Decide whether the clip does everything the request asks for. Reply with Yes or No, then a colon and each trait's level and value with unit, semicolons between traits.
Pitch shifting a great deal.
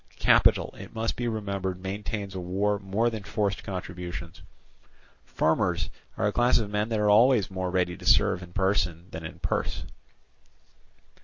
No: average, 2.7 semitones